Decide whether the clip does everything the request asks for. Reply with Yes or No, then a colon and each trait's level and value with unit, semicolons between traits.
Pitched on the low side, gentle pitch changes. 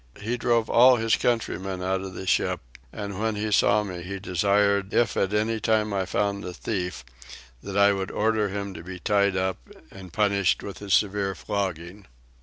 Yes: low, 100 Hz; narrow, 1.9 semitones